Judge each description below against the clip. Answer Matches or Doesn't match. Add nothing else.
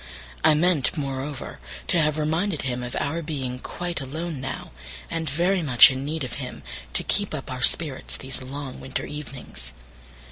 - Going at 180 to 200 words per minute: Doesn't match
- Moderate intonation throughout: Matches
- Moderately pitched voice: Matches